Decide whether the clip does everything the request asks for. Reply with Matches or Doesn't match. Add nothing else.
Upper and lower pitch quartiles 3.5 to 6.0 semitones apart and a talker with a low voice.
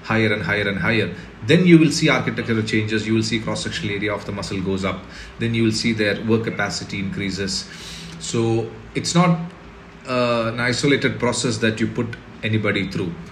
Doesn't match